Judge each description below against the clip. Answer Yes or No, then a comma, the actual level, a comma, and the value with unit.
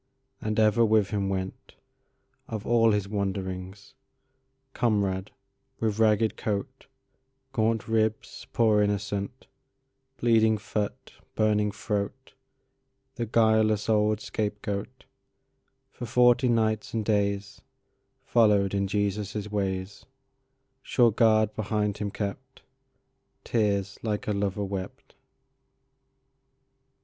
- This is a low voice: Yes, low, 110 Hz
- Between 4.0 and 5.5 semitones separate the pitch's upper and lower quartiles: No, average, 3.3 semitones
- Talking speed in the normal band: No, slow, 75 wpm